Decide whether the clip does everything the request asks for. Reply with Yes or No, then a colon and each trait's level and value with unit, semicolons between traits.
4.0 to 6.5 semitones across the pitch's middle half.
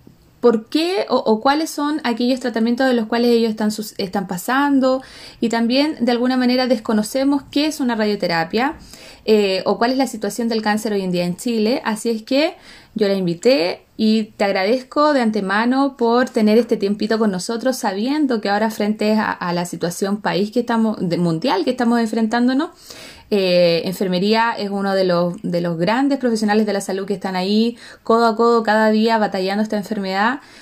No: average, 3.5 semitones